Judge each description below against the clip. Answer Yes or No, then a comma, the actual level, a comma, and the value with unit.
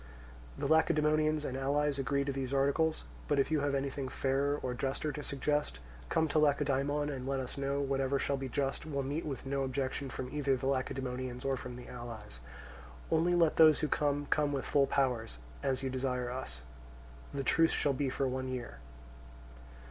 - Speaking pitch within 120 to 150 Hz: Yes, low, 135 Hz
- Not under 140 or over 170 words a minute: No, average, 185 wpm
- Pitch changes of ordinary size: No, narrow, 1.9 semitones